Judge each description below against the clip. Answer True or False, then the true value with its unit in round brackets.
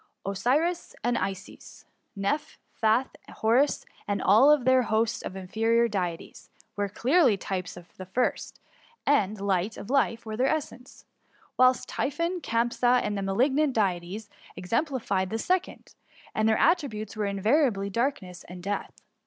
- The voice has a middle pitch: False (220 Hz)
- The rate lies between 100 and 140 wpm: True (135 wpm)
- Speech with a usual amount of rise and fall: True (4.8 semitones)